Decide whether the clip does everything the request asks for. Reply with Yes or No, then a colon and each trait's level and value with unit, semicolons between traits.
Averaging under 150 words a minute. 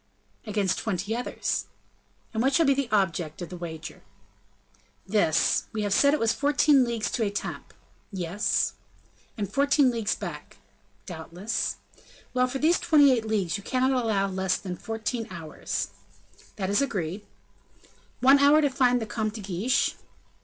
No: average, 155 wpm